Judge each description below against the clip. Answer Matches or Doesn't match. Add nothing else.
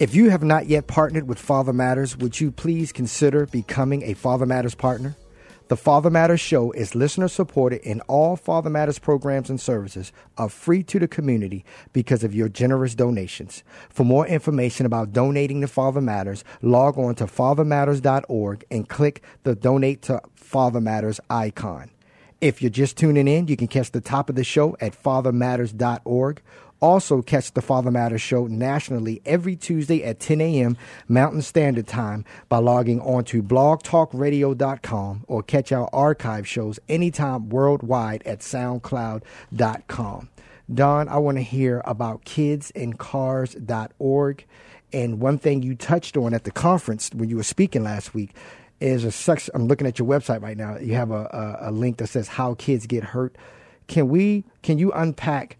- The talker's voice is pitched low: Matches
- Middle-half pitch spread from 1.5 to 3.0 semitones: Doesn't match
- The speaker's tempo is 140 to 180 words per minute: Matches